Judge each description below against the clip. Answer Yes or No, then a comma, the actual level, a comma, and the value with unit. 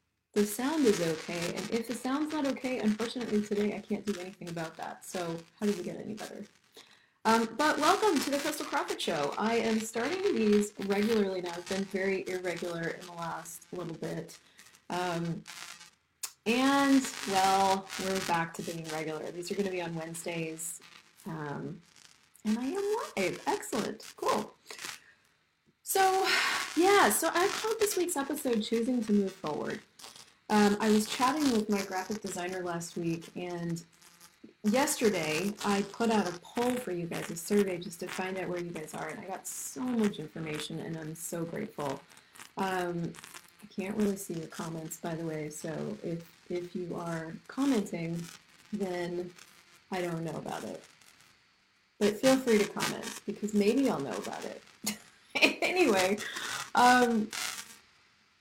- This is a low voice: No, high, 200 Hz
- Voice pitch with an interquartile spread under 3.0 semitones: No, average, 5.0 semitones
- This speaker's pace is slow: No, average, 160 wpm